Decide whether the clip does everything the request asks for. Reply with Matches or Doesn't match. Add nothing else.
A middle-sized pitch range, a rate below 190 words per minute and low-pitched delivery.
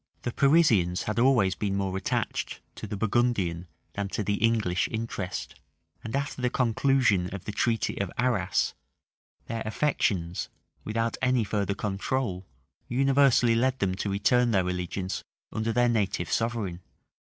Matches